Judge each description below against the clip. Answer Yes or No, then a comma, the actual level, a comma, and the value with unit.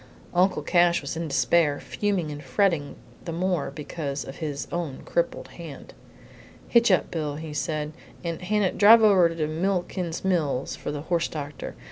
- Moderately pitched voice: Yes, medium, 165 Hz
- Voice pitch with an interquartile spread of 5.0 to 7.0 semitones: No, average, 3.6 semitones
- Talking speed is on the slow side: No, average, 165 wpm